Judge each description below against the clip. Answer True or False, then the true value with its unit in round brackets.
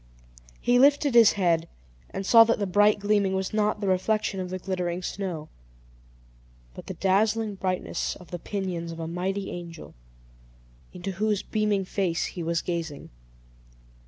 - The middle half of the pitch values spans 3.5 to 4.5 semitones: False (3.0 semitones)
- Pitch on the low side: False (190 Hz)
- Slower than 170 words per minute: True (155 wpm)